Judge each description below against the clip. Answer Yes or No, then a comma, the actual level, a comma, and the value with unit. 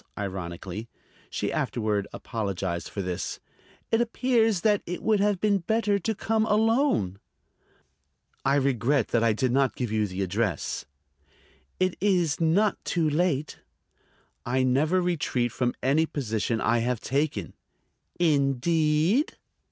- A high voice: No, medium, 140 Hz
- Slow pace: Yes, slow, 125 wpm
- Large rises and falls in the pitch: Yes, wide, 8.6 semitones